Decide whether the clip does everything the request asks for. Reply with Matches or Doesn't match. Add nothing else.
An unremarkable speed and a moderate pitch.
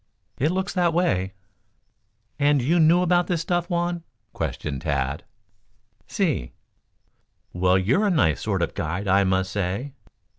Doesn't match